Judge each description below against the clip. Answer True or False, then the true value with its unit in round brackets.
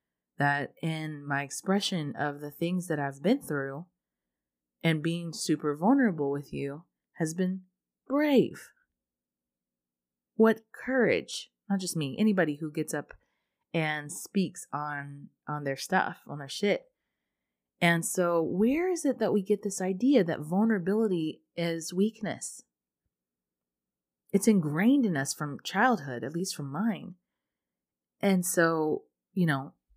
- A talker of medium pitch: True (160 Hz)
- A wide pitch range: True (6.0 semitones)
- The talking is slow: True (130 wpm)